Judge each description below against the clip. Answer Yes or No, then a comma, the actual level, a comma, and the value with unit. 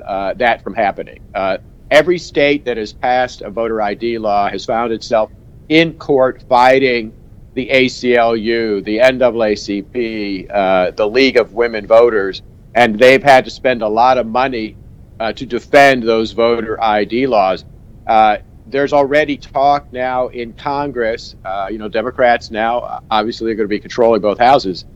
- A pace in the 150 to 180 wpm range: Yes, average, 160 wpm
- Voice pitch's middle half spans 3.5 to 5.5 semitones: No, average, 2.9 semitones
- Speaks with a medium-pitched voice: No, low, 115 Hz